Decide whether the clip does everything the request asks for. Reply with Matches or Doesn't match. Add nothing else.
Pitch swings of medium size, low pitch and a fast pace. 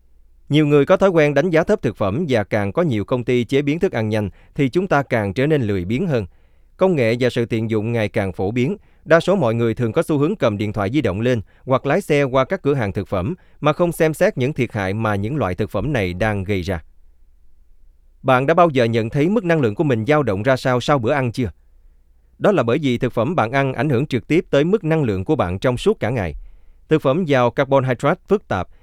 Doesn't match